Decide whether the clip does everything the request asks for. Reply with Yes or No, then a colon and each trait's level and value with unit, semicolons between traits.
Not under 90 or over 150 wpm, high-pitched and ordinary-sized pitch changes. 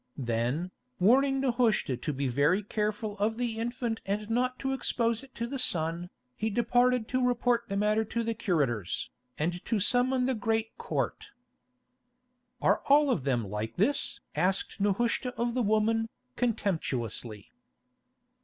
No: average, 145 wpm; high, 220 Hz; wide, 5.8 semitones